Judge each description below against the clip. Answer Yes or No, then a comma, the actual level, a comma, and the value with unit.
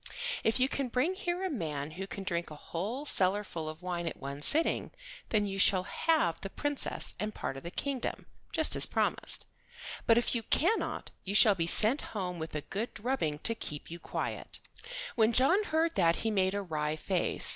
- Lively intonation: Yes, wide, 7.1 semitones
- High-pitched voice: Yes, high, 200 Hz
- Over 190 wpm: Yes, average, 200 wpm